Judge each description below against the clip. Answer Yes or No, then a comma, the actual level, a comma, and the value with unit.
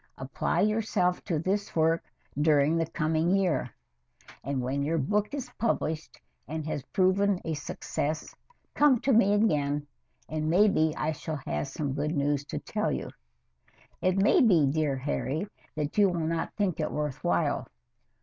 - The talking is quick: No, average, 160 wpm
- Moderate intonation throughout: Yes, average, 4.8 semitones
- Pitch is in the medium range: Yes, medium, 160 Hz